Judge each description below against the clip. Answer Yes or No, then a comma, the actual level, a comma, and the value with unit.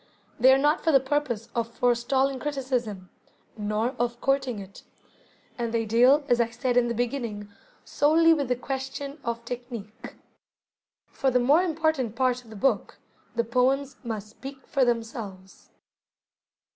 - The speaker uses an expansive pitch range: No, average, 2.9 semitones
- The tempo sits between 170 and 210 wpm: No, average, 150 wpm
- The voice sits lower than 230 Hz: No, high, 245 Hz